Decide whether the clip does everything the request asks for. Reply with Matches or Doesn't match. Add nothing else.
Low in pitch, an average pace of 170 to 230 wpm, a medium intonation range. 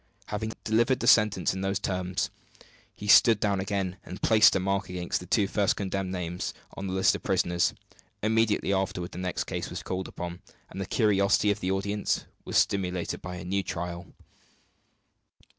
Doesn't match